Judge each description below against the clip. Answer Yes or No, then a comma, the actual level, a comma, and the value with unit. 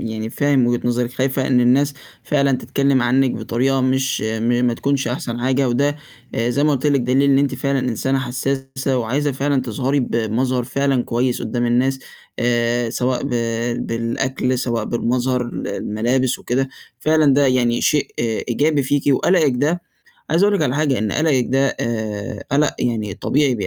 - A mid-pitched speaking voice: No, low, 130 Hz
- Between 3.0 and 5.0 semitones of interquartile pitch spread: No, narrow, 2.5 semitones